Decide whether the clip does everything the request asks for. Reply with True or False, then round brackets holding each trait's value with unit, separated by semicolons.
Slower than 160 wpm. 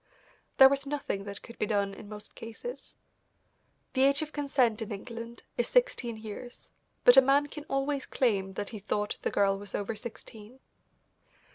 False (170 wpm)